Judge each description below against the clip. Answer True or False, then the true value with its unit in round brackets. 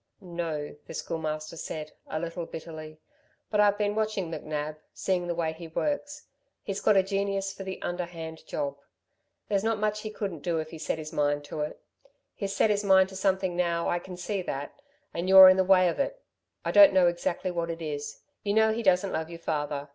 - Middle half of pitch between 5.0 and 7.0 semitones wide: False (3.7 semitones)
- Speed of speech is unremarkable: False (210 wpm)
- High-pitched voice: False (175 Hz)